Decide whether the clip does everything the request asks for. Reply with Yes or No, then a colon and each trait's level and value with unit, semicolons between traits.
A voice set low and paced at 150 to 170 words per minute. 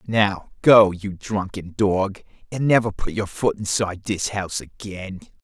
Yes: low, 100 Hz; average, 155 wpm